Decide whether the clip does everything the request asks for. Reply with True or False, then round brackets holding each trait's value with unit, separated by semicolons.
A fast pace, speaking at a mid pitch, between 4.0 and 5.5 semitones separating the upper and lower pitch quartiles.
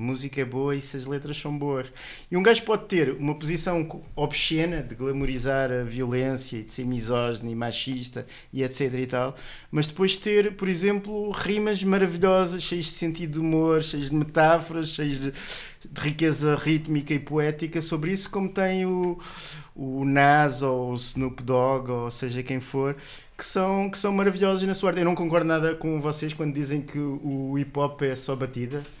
True (190 wpm; 150 Hz; 4.5 semitones)